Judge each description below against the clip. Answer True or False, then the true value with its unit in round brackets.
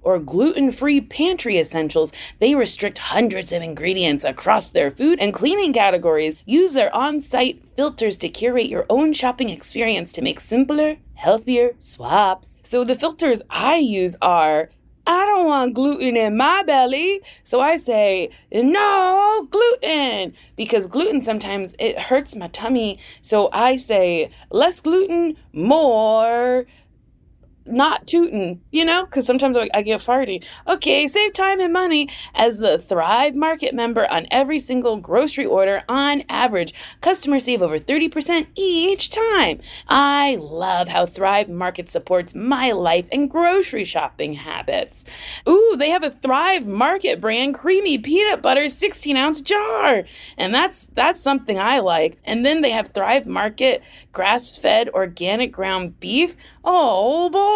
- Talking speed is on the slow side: False (145 wpm)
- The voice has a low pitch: False (260 Hz)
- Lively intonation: True (7.6 semitones)